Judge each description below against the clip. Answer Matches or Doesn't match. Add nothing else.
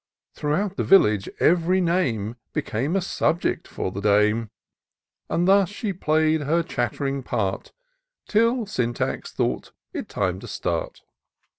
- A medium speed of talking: Doesn't match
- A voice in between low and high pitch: Matches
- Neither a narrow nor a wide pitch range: Doesn't match